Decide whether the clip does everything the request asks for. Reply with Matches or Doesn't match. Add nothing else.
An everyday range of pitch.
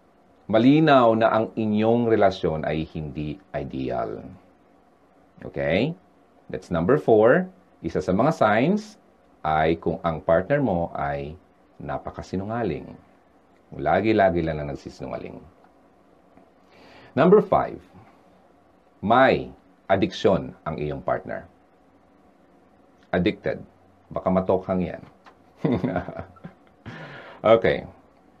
Doesn't match